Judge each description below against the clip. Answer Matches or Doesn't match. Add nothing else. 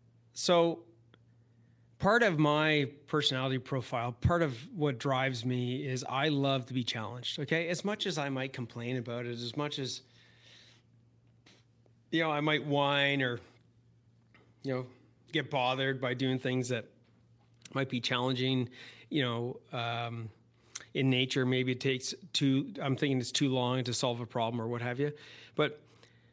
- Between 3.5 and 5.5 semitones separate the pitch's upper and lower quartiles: Doesn't match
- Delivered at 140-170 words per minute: Matches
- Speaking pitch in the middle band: Doesn't match